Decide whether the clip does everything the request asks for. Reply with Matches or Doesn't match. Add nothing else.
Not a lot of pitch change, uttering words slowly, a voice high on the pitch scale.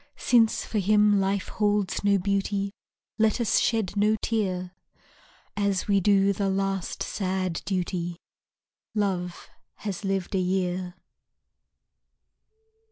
Matches